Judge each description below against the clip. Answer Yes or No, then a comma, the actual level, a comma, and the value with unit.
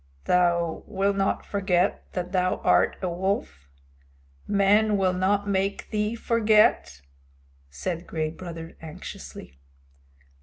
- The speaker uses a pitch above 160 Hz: Yes, medium, 185 Hz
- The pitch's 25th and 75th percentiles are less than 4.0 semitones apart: Yes, average, 2.8 semitones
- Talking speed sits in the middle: No, slow, 110 wpm